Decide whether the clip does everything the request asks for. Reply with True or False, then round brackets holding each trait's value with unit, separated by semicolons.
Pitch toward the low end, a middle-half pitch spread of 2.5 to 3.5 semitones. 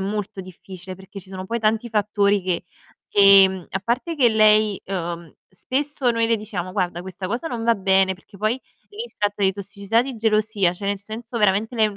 False (205 Hz; 2.9 semitones)